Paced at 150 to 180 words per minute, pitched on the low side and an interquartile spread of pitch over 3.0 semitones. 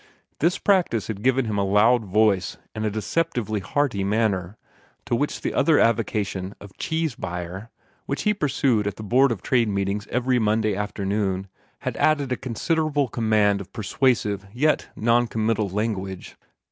Yes: average, 160 wpm; low, 110 Hz; average, 4.2 semitones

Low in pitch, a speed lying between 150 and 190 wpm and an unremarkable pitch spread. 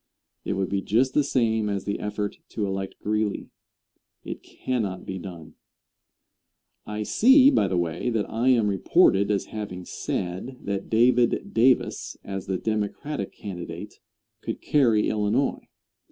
No: low, 105 Hz; average, 140 wpm; average, 3.5 semitones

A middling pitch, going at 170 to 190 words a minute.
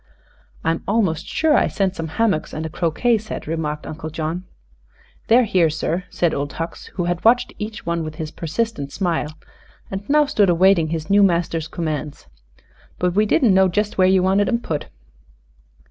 Yes: medium, 175 Hz; average, 175 wpm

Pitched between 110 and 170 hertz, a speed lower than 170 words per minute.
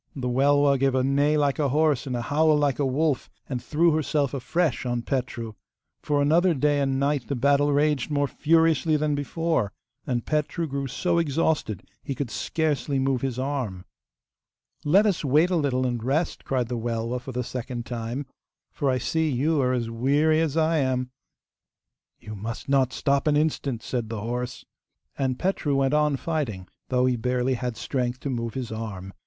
No: low, 135 Hz; average, 185 wpm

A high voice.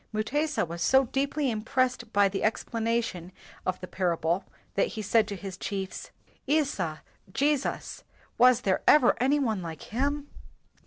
Yes: high, 225 Hz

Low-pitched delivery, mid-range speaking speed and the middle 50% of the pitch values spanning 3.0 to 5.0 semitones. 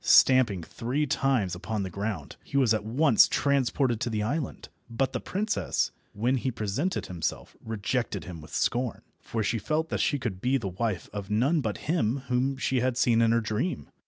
Yes: low, 115 Hz; average, 190 wpm; average, 4.3 semitones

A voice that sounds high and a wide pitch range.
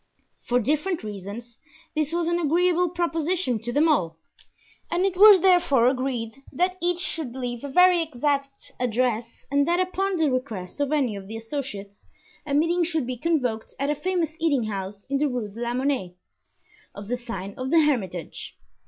Yes: very high, 275 Hz; wide, 6.2 semitones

